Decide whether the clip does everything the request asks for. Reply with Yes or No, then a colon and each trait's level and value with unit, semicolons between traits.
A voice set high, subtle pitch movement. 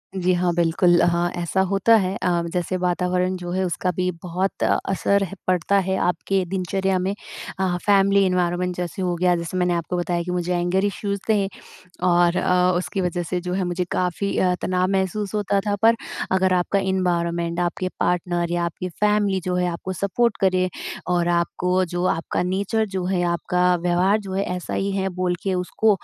No: medium, 180 Hz; narrow, 1.5 semitones